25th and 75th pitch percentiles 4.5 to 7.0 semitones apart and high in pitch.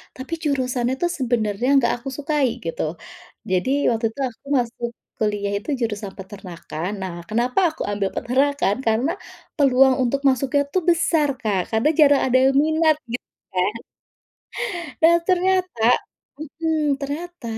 Yes: average, 5.2 semitones; very high, 255 Hz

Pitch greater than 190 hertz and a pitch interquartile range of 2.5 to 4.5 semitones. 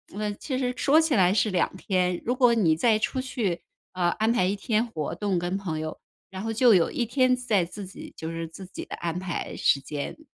No: high, 200 Hz; average, 5.2 semitones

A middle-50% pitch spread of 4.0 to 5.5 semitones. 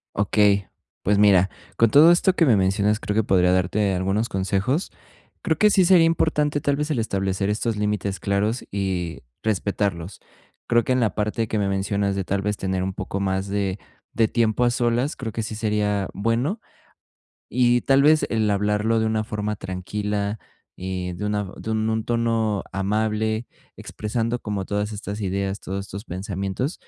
No: average, 2.7 semitones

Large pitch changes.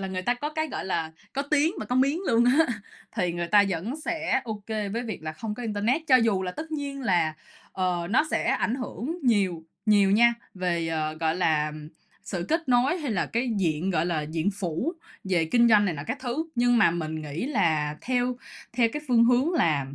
Yes: wide, 6.6 semitones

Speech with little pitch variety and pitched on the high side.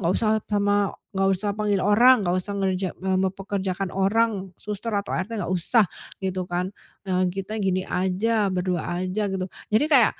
Yes: narrow, 2.1 semitones; high, 195 Hz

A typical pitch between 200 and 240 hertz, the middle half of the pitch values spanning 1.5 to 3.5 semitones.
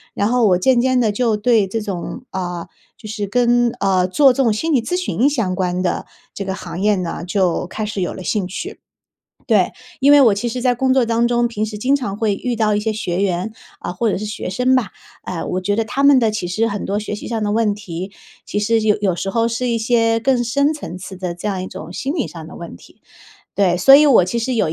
No: high, 215 Hz; average, 4.3 semitones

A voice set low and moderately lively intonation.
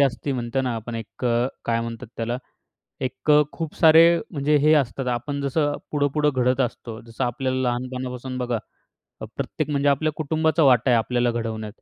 Yes: low, 130 Hz; average, 3.3 semitones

